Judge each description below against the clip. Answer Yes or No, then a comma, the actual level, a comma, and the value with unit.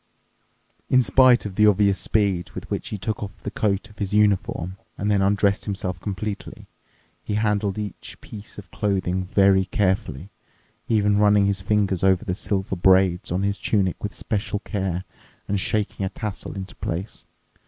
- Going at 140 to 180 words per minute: Yes, average, 165 wpm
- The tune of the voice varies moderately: No, narrow, 1.7 semitones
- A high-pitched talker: No, low, 100 Hz